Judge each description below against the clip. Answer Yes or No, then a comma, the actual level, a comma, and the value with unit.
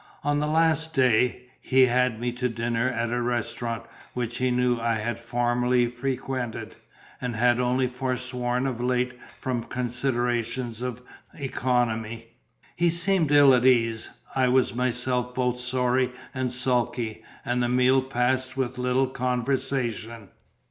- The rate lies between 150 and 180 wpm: No, average, 140 wpm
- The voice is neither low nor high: No, low, 125 Hz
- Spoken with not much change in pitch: Yes, narrow, 1.3 semitones